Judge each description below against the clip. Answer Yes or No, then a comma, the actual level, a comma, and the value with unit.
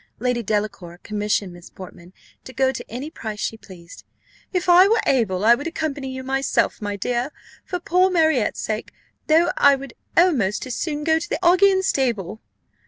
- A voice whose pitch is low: No, very high, 260 Hz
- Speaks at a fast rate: No, average, 175 wpm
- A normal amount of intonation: No, wide, 7.2 semitones